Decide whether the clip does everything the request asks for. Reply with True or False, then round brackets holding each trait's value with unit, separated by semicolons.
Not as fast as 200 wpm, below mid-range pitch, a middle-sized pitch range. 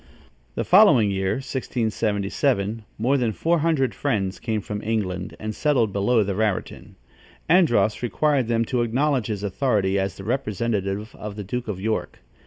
True (155 wpm; 110 Hz; 3.7 semitones)